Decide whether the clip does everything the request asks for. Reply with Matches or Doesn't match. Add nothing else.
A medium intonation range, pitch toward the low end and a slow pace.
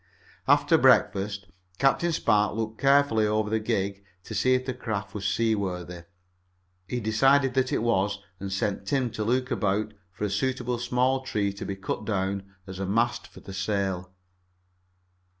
Doesn't match